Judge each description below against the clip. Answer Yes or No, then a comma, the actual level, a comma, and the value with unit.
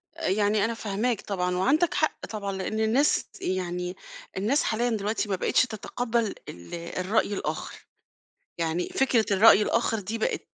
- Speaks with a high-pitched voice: Yes, high, 210 Hz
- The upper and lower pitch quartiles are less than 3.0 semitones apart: No, average, 3.4 semitones